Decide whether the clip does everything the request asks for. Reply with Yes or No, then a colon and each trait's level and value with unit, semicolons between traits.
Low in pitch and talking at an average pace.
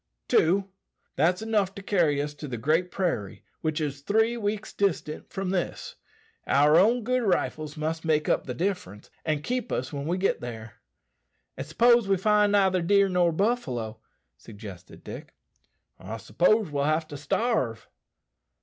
No: medium, 170 Hz; average, 160 wpm